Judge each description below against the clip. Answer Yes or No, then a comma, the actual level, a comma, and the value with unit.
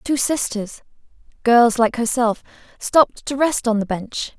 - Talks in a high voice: Yes, high, 240 Hz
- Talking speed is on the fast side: No, average, 150 wpm